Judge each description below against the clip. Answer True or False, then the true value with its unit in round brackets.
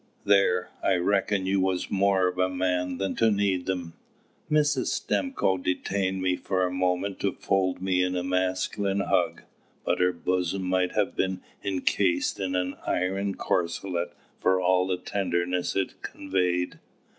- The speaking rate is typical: True (155 wpm)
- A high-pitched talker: False (95 Hz)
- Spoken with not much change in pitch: True (1.2 semitones)